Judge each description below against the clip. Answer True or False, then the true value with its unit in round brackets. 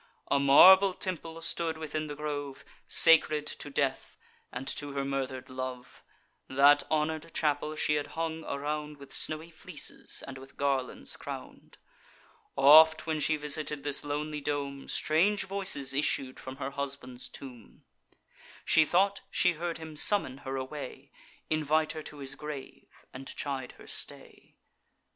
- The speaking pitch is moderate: True (145 Hz)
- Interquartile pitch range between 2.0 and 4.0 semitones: True (2.4 semitones)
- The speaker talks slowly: False (145 wpm)